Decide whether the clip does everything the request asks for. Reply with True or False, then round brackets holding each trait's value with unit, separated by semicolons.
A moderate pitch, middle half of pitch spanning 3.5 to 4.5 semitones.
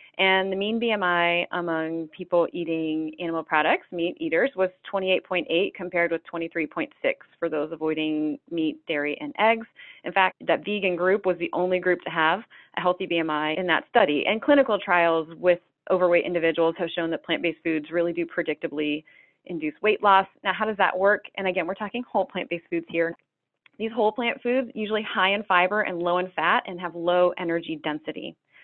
False (175 Hz; 2.8 semitones)